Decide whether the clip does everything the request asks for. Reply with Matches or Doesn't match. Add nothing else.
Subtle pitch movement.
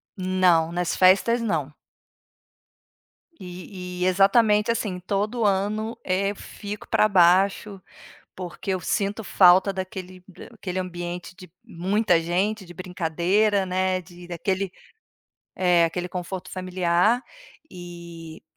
Matches